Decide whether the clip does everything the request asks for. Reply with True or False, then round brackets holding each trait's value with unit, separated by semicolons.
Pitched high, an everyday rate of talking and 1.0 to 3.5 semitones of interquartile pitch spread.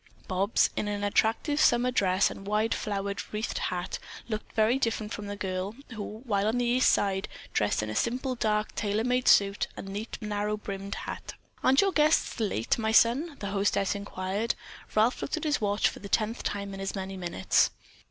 True (210 Hz; 195 wpm; 2.8 semitones)